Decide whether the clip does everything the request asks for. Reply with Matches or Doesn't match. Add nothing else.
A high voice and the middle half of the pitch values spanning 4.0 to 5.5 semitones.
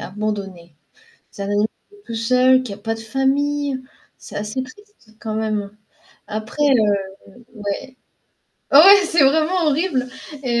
Matches